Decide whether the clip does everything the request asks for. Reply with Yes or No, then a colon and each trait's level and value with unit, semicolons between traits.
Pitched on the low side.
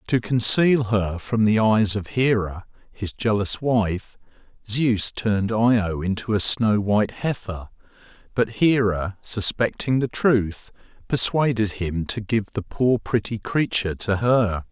Yes: low, 110 Hz